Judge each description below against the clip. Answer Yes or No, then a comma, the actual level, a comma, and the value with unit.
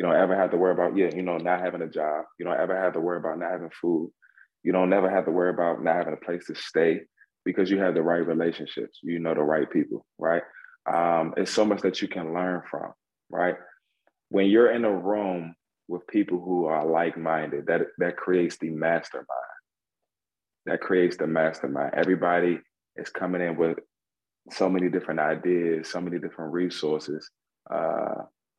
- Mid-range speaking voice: No, very low, 85 Hz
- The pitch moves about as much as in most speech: No, narrow, 1.7 semitones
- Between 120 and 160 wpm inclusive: No, average, 195 wpm